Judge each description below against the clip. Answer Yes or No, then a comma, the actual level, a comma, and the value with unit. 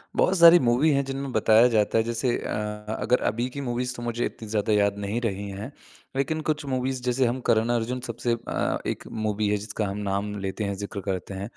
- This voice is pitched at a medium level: No, low, 115 Hz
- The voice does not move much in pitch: No, average, 3.3 semitones